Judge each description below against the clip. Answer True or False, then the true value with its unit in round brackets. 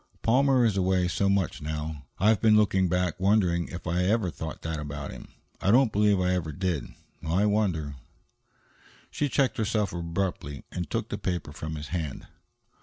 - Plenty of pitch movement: False (4.5 semitones)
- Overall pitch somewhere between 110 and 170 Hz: False (90 Hz)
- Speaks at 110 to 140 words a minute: False (180 wpm)